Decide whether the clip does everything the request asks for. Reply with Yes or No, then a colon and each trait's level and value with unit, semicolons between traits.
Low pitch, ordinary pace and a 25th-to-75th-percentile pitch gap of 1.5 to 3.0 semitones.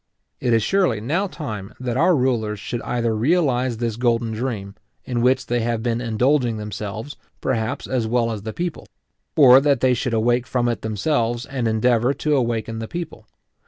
Yes: low, 120 Hz; average, 180 wpm; average, 2.7 semitones